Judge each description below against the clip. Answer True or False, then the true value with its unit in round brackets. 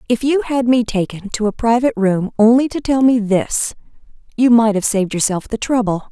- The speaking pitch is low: False (230 Hz)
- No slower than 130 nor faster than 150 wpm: False (205 wpm)